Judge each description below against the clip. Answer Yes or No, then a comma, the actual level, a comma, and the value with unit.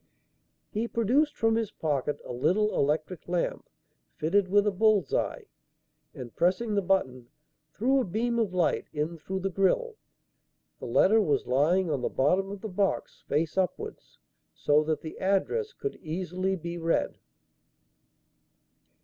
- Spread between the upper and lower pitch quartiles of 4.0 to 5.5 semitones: Yes, average, 5.2 semitones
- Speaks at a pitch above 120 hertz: Yes, medium, 185 Hz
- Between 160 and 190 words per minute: No, average, 150 wpm